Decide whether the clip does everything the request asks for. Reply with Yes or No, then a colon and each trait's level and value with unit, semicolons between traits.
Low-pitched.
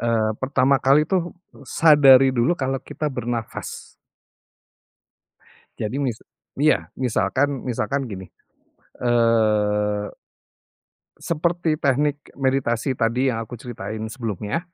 Yes: low, 130 Hz